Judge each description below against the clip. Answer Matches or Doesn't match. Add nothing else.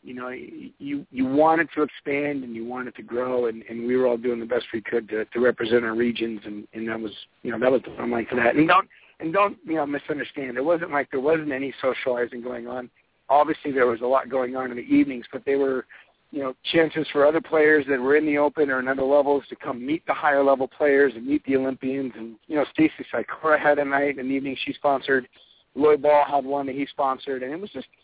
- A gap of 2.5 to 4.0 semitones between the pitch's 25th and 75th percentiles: Matches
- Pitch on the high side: Doesn't match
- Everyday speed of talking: Doesn't match